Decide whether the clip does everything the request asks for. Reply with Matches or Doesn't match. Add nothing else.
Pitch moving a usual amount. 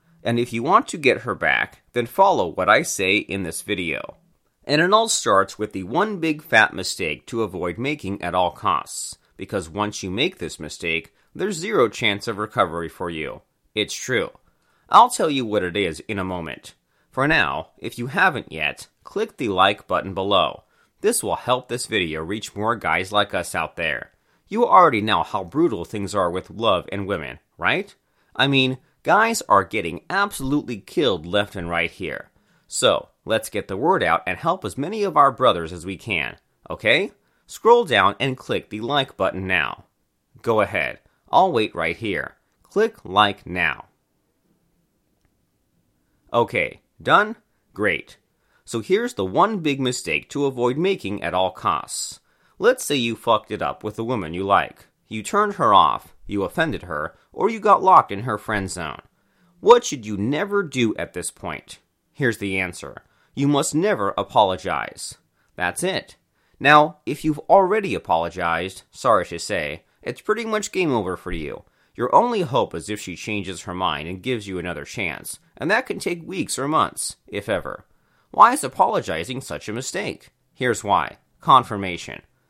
Doesn't match